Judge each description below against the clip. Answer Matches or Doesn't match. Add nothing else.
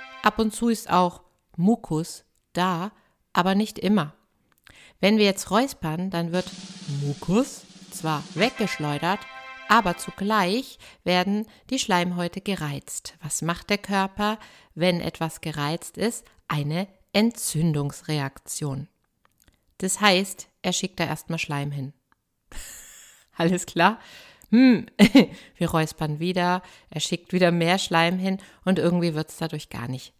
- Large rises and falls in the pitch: Doesn't match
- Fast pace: Doesn't match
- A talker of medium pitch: Matches